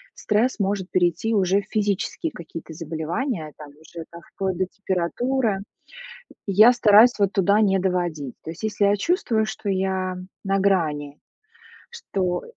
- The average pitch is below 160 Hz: No, high, 190 Hz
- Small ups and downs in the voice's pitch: No, average, 3.6 semitones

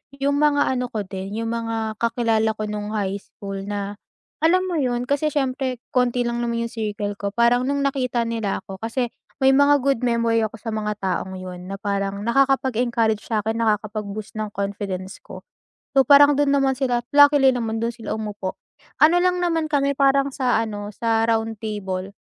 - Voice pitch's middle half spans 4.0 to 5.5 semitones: Yes, average, 4.3 semitones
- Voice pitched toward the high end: Yes, high, 230 Hz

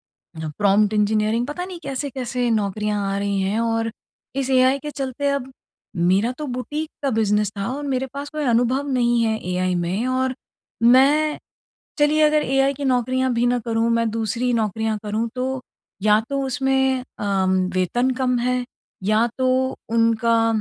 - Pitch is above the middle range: Yes, high, 245 Hz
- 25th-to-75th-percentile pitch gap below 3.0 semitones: No, average, 3.6 semitones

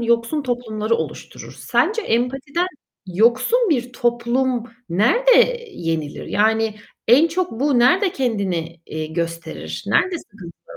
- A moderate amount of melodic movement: No, wide, 6.0 semitones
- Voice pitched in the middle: No, high, 240 Hz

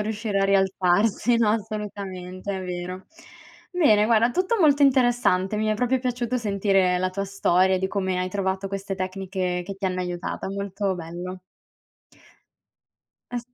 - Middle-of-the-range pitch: No, high, 195 Hz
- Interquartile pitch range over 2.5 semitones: Yes, average, 2.9 semitones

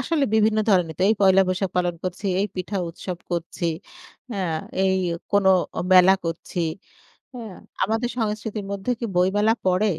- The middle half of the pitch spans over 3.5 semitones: No, average, 2.9 semitones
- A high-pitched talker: Yes, high, 195 Hz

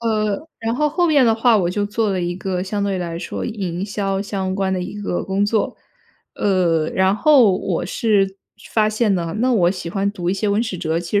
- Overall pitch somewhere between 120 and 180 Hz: No, high, 200 Hz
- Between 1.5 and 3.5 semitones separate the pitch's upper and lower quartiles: Yes, average, 2.8 semitones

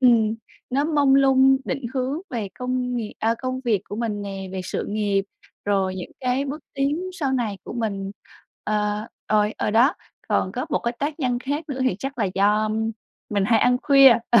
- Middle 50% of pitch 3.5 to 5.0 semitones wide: Yes, average, 4.3 semitones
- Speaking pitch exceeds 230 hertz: Yes, high, 240 Hz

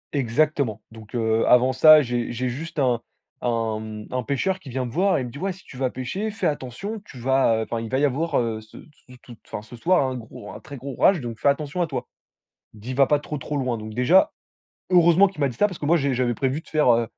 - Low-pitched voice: Yes, low, 130 Hz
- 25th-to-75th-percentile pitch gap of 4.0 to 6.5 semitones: Yes, average, 4.4 semitones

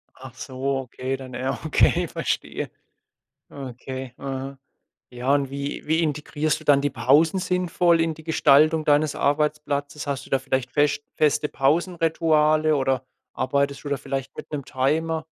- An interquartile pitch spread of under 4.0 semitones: Yes, narrow, 2.6 semitones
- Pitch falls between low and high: Yes, medium, 145 Hz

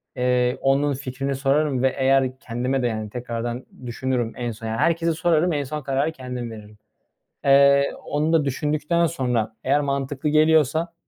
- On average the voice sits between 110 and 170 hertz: Yes, low, 135 Hz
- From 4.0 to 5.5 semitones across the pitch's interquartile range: No, average, 3.0 semitones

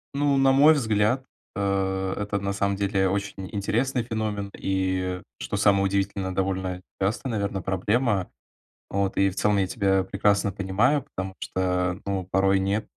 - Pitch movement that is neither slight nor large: No, narrow, 1.9 semitones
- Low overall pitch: Yes, low, 100 Hz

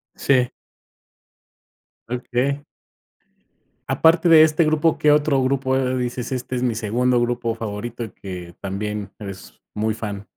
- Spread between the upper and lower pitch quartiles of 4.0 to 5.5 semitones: Yes, average, 4.4 semitones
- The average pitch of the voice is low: Yes, low, 125 Hz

